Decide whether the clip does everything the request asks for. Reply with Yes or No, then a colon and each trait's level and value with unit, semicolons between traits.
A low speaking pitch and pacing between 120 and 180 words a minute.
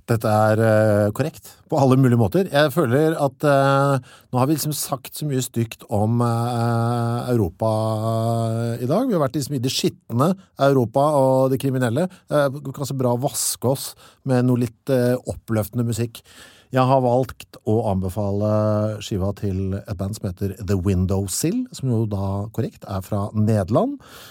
Yes: low, 120 Hz; average, 170 wpm